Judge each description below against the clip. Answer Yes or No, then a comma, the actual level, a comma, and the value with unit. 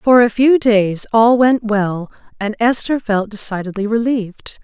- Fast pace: No, average, 155 wpm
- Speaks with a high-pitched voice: Yes, high, 220 Hz